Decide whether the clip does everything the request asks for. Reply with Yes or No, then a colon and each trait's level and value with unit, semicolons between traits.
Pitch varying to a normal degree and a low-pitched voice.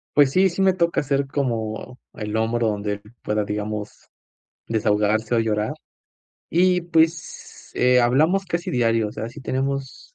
No: wide, 6.8 semitones; low, 125 Hz